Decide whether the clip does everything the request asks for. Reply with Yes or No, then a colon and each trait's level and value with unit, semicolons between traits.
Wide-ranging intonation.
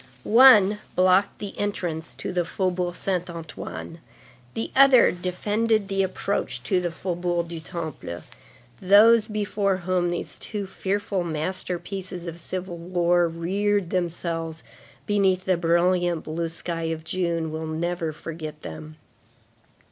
No: average, 2.7 semitones